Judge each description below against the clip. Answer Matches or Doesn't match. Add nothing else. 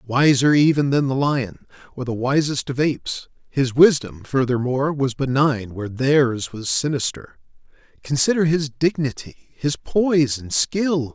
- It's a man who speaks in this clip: Matches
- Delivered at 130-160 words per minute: Matches